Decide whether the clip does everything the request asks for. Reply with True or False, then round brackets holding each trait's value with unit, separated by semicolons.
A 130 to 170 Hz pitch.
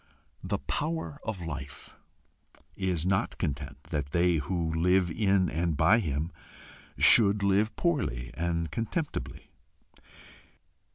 False (85 Hz)